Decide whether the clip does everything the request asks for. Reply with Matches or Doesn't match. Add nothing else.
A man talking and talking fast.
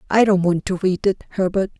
Doesn't match